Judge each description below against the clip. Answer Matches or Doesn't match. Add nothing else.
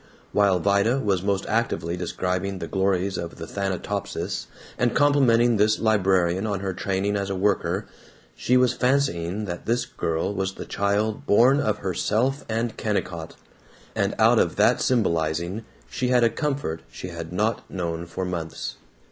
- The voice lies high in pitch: Doesn't match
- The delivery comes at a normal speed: Matches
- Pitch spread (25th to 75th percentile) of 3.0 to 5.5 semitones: Matches